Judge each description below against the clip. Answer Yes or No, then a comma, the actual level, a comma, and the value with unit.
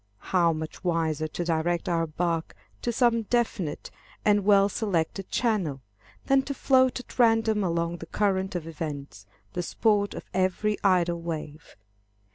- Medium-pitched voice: Yes, medium, 180 Hz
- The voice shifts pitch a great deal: No, average, 4.4 semitones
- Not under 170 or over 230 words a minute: No, average, 145 wpm